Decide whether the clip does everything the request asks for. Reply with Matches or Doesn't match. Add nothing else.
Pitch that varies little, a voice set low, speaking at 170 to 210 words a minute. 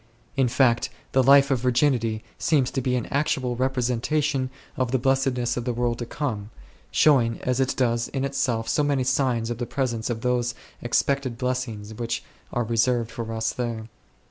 Matches